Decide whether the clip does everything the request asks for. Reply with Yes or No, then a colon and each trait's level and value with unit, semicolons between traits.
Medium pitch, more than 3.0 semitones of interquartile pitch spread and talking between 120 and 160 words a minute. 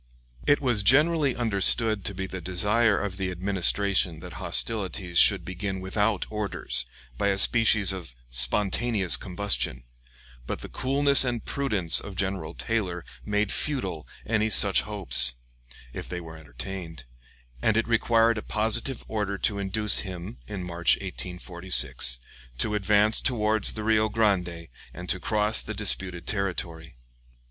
No: low, 100 Hz; average, 3.4 semitones; average, 140 wpm